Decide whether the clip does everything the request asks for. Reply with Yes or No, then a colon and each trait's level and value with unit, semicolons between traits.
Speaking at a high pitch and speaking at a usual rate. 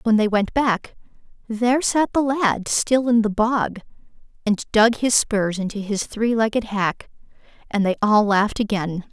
Yes: high, 220 Hz; average, 170 wpm